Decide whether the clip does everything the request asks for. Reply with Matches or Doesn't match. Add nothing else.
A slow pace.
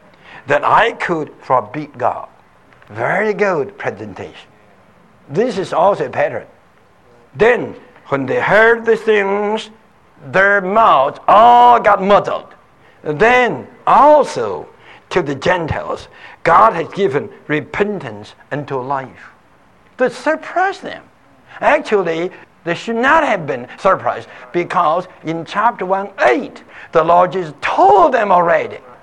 Matches